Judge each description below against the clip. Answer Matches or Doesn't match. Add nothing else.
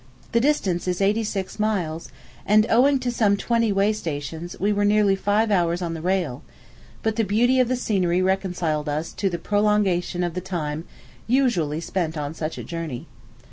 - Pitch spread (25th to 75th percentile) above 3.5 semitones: Matches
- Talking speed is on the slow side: Doesn't match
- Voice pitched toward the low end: Doesn't match